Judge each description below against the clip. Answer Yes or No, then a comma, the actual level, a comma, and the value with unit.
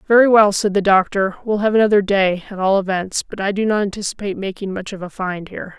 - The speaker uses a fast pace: Yes, fast, 240 wpm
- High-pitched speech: Yes, high, 200 Hz